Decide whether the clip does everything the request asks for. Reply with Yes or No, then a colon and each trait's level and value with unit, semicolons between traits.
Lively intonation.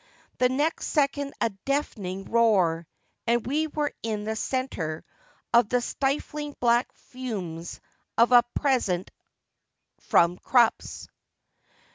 Yes: wide, 5.9 semitones